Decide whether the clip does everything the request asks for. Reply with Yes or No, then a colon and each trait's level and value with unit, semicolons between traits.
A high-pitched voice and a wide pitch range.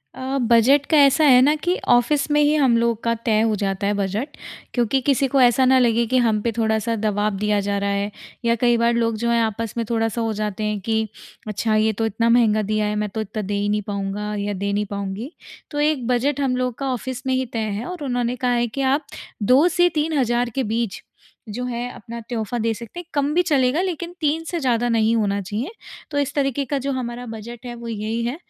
No: high, 235 Hz; average, 3.6 semitones